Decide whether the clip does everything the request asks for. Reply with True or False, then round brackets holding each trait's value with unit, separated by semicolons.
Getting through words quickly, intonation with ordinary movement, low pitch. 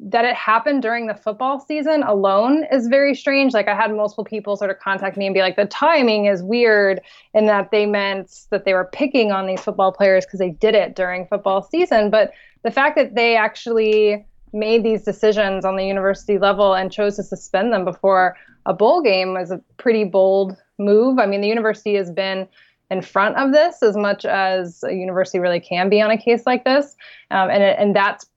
False (215 wpm; 3.0 semitones; 205 Hz)